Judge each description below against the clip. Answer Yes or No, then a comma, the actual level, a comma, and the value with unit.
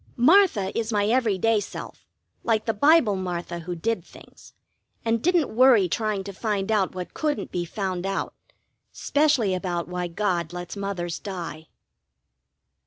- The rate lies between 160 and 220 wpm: No, average, 150 wpm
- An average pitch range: Yes, average, 4.1 semitones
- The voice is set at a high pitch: Yes, high, 200 Hz